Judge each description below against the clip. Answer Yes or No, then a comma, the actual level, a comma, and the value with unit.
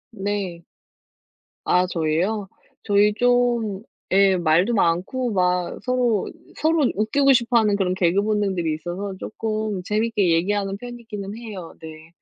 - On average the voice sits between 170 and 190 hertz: No, high, 200 Hz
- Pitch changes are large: No, average, 3.7 semitones